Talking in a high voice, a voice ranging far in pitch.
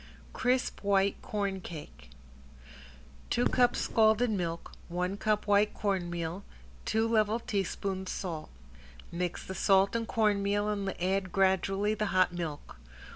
No: high, 195 Hz; average, 2.8 semitones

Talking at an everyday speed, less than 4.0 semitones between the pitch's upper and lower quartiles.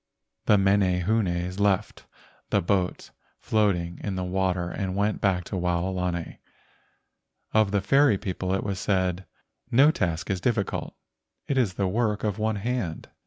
Yes: average, 145 wpm; narrow, 2.6 semitones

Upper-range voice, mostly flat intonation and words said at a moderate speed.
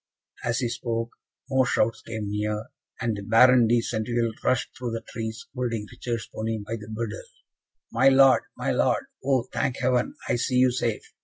No: low, 115 Hz; narrow, 2.2 semitones; average, 175 wpm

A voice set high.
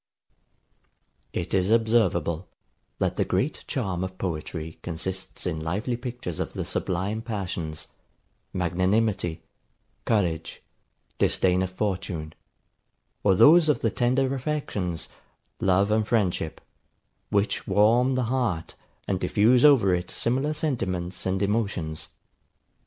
No: very low, 95 Hz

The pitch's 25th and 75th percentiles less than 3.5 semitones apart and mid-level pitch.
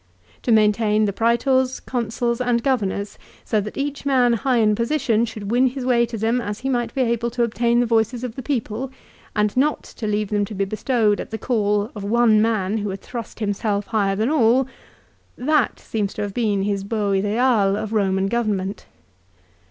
No: average, 2.7 semitones; high, 225 Hz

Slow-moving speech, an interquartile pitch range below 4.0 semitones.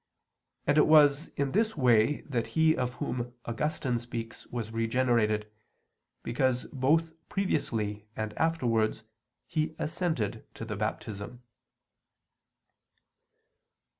No: slow, 105 wpm; average, 5.2 semitones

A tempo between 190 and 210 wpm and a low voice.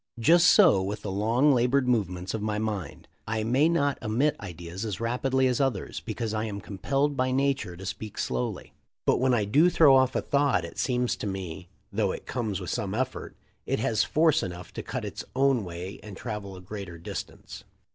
Yes: average, 200 wpm; low, 110 Hz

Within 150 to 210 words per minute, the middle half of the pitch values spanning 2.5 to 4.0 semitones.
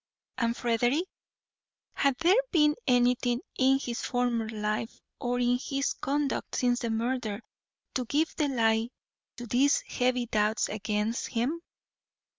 No: slow, 135 wpm; average, 2.9 semitones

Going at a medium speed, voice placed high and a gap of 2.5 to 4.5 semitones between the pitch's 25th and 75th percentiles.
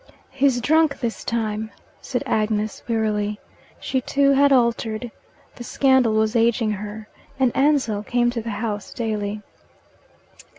No: slow, 130 wpm; high, 230 Hz; average, 3.2 semitones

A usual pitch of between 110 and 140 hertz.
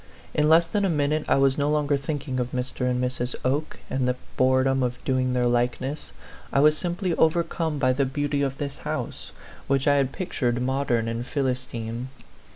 Yes: low, 135 Hz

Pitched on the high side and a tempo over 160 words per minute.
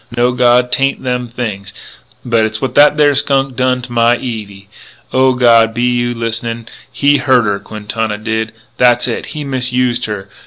No: low, 120 Hz; average, 170 wpm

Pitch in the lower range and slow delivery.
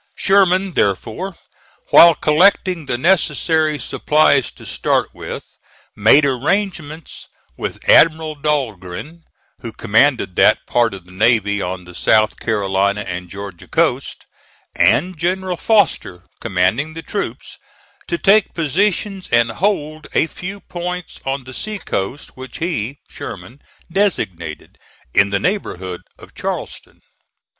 No: medium, 145 Hz; slow, 120 wpm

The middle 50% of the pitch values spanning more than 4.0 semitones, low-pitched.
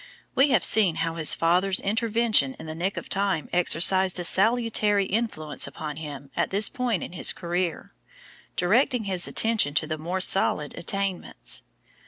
No: average, 4.6 semitones; medium, 185 Hz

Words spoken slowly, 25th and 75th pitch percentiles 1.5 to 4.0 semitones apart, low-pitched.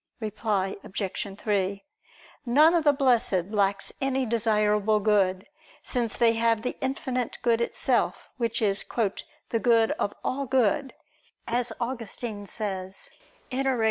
No: slow, 125 wpm; average, 3.5 semitones; high, 225 Hz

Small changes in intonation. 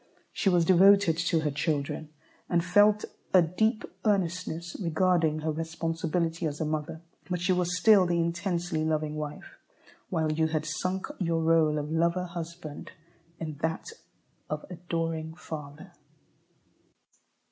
Yes: narrow, 2.3 semitones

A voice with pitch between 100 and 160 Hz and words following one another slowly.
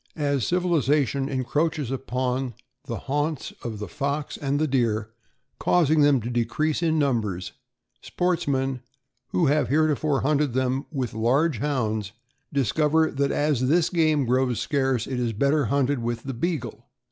No: medium, 140 Hz; average, 145 wpm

